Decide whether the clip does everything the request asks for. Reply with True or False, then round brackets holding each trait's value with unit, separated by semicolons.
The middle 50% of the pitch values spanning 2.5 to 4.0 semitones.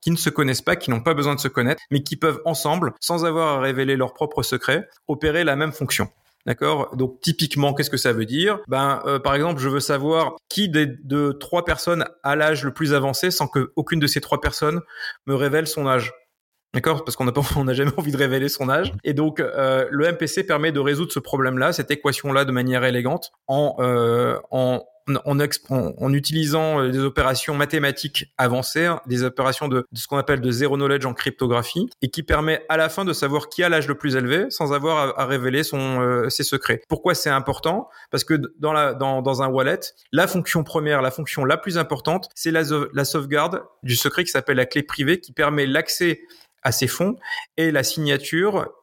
True (2.9 semitones)